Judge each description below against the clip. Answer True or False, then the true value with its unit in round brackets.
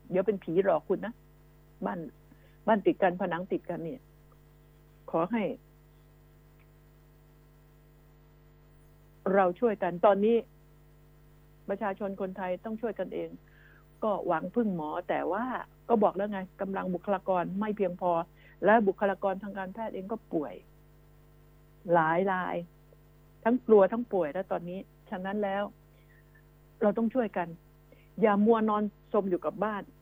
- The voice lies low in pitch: False (185 Hz)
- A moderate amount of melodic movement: True (5.0 semitones)